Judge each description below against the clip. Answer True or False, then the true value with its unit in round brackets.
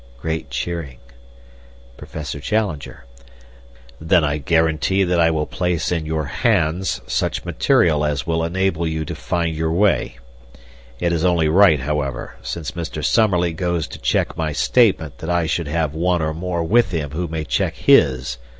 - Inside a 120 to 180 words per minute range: True (160 wpm)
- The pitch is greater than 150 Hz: False (80 Hz)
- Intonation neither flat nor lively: False (2.3 semitones)